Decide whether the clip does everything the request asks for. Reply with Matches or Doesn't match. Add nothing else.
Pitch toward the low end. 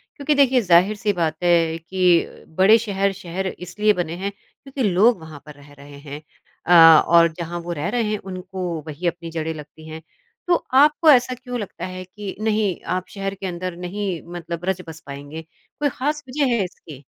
Doesn't match